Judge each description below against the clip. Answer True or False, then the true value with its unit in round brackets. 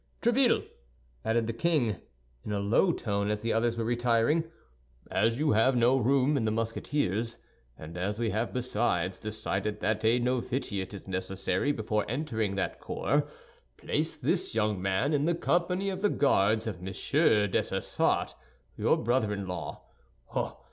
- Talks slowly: False (155 wpm)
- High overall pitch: False (115 Hz)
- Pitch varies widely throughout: False (4.3 semitones)